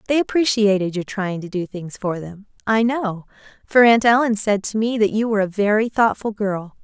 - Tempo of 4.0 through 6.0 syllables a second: Yes, 5.1 syllables/s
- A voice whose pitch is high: Yes, high, 210 Hz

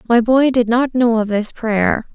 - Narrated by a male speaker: No, female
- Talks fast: Yes, fast, 225 wpm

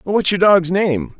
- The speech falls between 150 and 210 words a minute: Yes, average, 200 wpm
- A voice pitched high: No, medium, 180 Hz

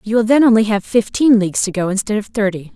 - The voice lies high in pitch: Yes, high, 215 Hz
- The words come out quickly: Yes, fast, 260 wpm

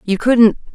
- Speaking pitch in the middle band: No, high, 220 Hz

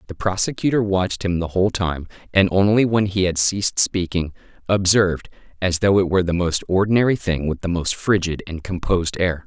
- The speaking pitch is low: Yes, very low, 95 Hz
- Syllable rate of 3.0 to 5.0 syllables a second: No, 5.7 syllables/s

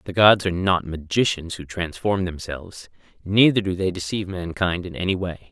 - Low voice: Yes, very low, 90 Hz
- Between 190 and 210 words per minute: No, average, 175 wpm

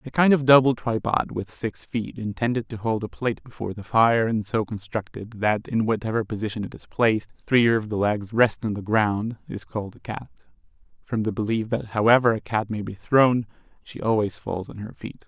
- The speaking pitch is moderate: No, low, 110 Hz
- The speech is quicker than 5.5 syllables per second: No, 5.3 syllables/s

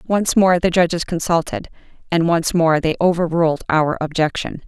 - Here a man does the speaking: No, female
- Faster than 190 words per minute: No, average, 155 wpm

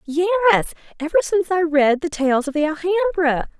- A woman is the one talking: Yes, female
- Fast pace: No, average, 165 wpm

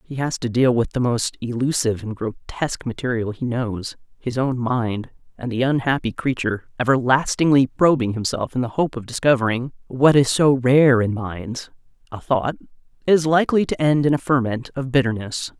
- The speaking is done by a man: No, female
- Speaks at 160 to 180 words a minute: Yes, average, 170 wpm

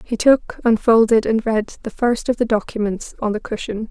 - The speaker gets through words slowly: No, average, 200 wpm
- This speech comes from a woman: Yes, female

